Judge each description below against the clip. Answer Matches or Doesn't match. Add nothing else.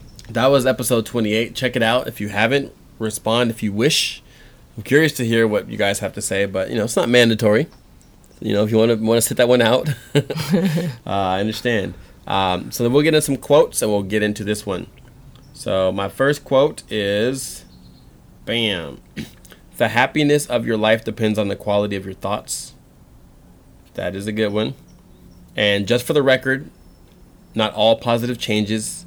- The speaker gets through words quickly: Doesn't match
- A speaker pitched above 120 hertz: Doesn't match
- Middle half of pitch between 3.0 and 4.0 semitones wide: Matches